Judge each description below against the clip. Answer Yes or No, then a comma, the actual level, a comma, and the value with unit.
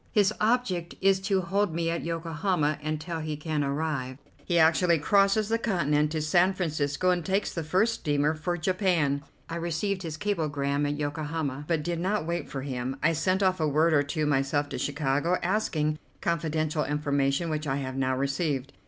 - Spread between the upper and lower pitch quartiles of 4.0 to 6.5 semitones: No, average, 3.5 semitones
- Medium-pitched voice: Yes, medium, 160 Hz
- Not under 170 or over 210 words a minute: Yes, average, 180 wpm